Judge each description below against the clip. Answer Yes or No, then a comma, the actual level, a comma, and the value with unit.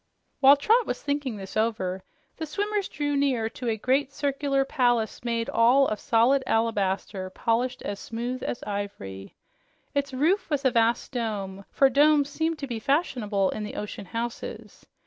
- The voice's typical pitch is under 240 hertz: No, high, 245 Hz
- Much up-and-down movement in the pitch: No, average, 4.5 semitones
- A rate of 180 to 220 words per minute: No, average, 165 wpm